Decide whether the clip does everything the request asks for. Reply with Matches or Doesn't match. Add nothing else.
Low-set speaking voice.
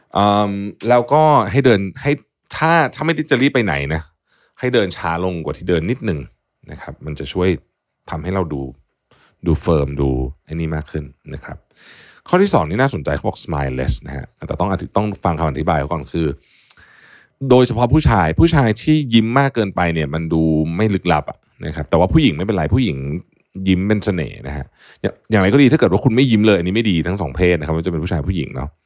Matches